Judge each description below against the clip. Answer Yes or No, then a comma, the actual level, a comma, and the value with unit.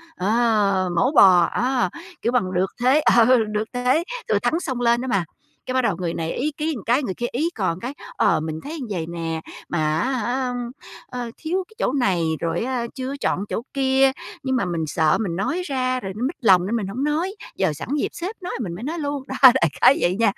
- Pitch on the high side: Yes, high, 240 Hz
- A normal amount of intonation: No, wide, 6.2 semitones